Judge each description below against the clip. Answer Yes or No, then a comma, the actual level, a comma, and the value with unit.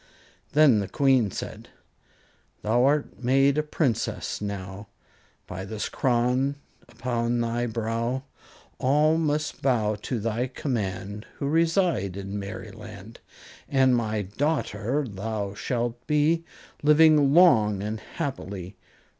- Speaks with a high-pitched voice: No, low, 120 Hz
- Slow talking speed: Yes, slow, 115 wpm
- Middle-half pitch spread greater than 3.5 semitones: Yes, average, 5.2 semitones